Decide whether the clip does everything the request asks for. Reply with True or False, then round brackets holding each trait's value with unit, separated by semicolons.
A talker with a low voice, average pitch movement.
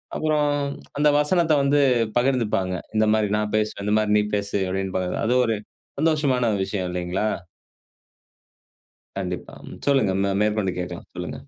False (105 Hz; 6.3 semitones)